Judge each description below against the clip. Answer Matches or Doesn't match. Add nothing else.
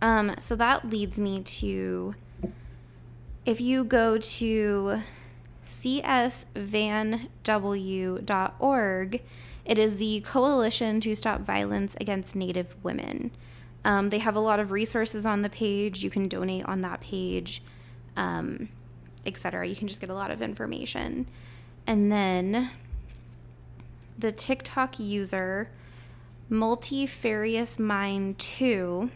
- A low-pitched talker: Doesn't match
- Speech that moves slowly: Matches